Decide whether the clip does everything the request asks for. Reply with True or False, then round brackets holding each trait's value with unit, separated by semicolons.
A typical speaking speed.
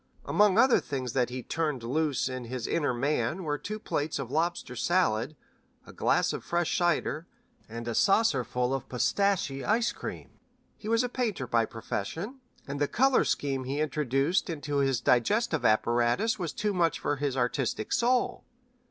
True (170 wpm)